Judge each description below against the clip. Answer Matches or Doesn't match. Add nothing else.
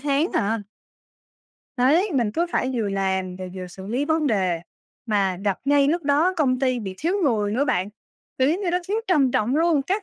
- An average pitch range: Doesn't match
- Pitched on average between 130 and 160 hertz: Doesn't match